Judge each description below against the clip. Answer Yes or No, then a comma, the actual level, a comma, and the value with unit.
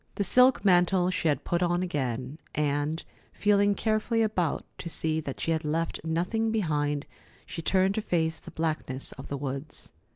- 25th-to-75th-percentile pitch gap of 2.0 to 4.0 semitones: No, average, 4.6 semitones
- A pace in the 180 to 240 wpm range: No, average, 165 wpm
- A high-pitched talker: No, medium, 165 Hz